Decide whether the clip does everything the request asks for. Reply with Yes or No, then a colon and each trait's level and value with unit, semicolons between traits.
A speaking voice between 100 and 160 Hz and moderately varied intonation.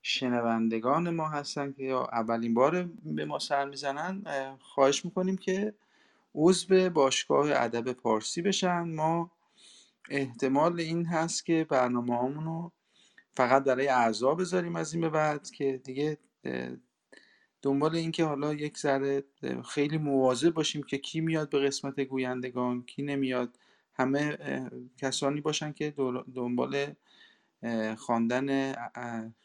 Yes: medium, 140 Hz; average, 4.2 semitones